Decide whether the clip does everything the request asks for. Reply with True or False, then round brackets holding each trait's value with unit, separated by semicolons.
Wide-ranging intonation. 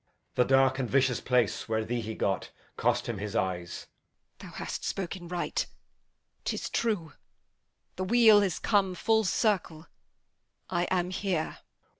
True (7.8 semitones)